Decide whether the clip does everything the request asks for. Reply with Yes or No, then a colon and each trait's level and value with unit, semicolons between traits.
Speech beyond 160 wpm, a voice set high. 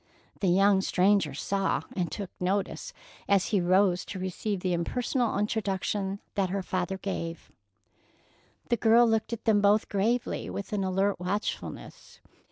No: average, 145 wpm; high, 195 Hz